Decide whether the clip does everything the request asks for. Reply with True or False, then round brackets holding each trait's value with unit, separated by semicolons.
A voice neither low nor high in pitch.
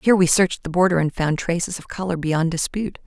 True (175 Hz)